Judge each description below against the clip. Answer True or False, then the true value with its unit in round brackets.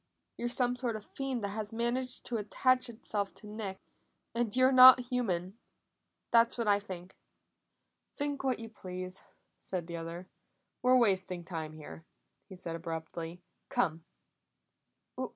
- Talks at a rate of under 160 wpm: True (145 wpm)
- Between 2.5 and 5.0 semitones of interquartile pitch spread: False (5.4 semitones)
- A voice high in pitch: True (210 Hz)